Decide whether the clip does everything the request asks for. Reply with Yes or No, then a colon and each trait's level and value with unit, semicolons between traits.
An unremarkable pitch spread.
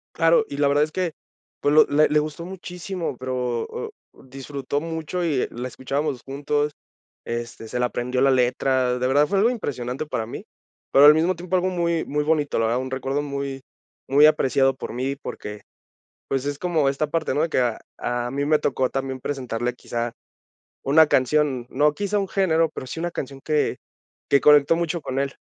Yes: average, 3.5 semitones